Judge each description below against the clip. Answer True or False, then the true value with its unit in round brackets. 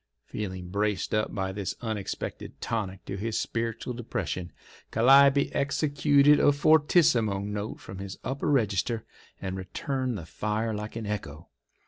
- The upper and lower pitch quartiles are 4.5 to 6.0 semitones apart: True (5.2 semitones)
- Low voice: True (110 Hz)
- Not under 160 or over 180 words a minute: False (135 wpm)